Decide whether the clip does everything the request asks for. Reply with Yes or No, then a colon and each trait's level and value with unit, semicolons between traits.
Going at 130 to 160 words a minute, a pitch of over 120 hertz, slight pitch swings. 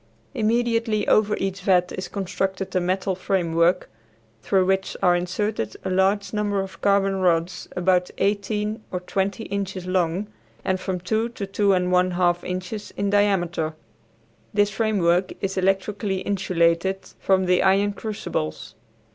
Yes: average, 140 wpm; high, 190 Hz; narrow, 1.9 semitones